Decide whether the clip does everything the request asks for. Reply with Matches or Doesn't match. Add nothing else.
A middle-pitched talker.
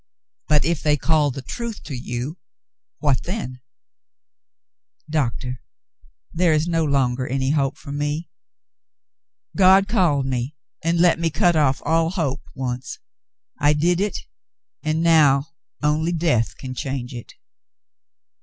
Matches